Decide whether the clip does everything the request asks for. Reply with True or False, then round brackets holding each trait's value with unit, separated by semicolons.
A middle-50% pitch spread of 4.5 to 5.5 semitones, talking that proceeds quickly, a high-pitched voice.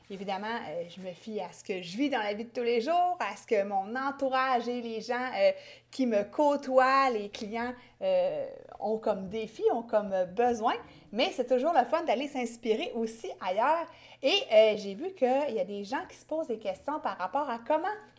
False (4.9 semitones; 200 wpm; 245 Hz)